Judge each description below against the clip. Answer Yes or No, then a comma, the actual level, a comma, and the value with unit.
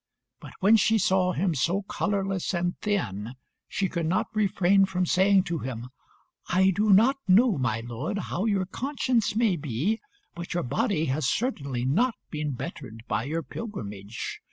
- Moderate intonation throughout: No, wide, 6.6 semitones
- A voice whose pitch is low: No, medium, 185 Hz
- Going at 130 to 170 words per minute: Yes, average, 160 wpm